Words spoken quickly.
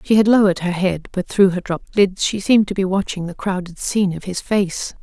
Yes: fast, 250 wpm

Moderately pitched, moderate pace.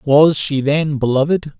Yes: medium, 145 Hz; average, 150 wpm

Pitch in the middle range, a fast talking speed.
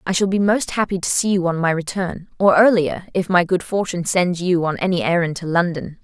Yes: medium, 180 Hz; fast, 230 wpm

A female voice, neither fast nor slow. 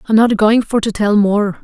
No: female; fast, 255 wpm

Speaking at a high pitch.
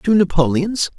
No: medium, 180 Hz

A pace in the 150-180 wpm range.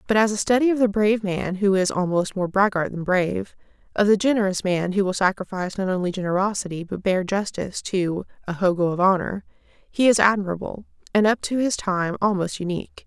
No: average, 195 wpm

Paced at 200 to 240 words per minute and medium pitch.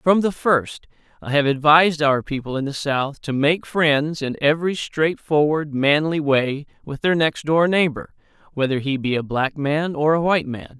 No: average, 190 wpm; medium, 150 Hz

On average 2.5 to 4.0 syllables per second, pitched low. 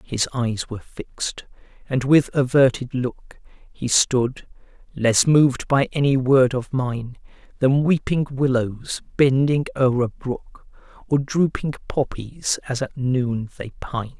Yes: 3.9 syllables/s; low, 130 Hz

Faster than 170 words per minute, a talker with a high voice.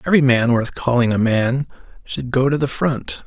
No: average, 200 wpm; low, 125 Hz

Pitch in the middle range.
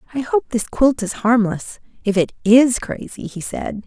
No: high, 230 Hz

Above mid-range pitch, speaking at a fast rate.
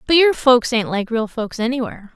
Yes: high, 240 Hz; fast, 225 wpm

